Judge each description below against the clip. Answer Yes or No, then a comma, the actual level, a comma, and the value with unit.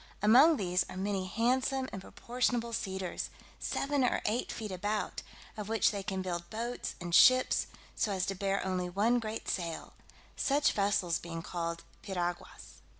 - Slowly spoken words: No, average, 155 wpm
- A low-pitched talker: No, high, 200 Hz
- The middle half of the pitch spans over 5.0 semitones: No, average, 4.3 semitones